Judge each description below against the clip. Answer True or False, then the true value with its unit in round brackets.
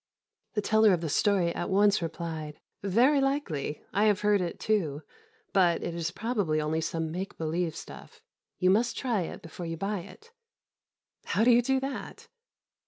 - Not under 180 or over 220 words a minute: False (170 wpm)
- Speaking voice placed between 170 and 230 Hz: True (190 Hz)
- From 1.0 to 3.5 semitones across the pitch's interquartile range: False (4.8 semitones)